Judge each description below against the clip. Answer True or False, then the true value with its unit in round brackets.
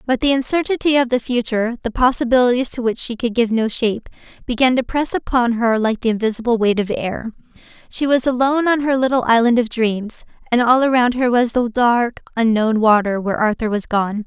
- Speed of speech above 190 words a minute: True (200 wpm)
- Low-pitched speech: False (240 Hz)